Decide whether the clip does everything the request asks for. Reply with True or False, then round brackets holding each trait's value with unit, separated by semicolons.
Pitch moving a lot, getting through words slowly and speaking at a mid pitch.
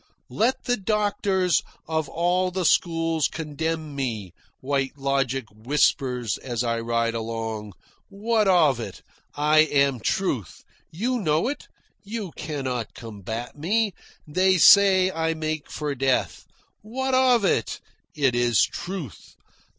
True (7.0 semitones; 125 wpm; 155 Hz)